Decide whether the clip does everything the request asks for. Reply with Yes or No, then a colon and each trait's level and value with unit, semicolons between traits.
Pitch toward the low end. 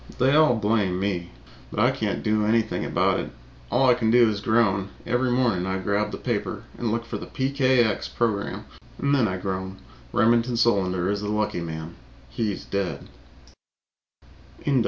Yes: low, 105 Hz